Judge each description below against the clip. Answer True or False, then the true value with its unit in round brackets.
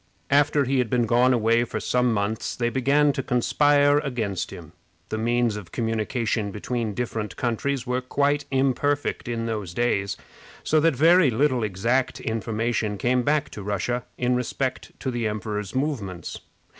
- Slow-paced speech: False (155 wpm)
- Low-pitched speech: True (120 Hz)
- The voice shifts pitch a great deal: False (3.5 semitones)